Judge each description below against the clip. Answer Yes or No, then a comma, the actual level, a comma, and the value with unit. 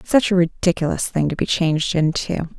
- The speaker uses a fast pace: No, average, 185 wpm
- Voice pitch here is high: No, medium, 170 Hz